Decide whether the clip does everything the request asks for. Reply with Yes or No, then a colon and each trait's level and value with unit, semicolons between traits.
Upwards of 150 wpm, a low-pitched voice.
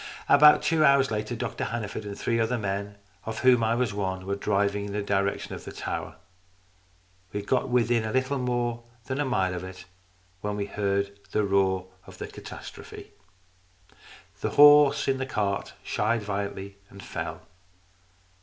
Yes: average, 170 wpm; low, 105 Hz